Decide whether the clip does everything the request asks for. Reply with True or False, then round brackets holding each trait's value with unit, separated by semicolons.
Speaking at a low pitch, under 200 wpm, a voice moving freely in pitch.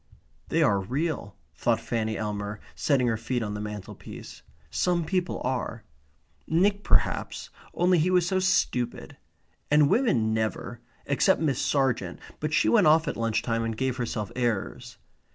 True (125 Hz; 155 wpm; 6.7 semitones)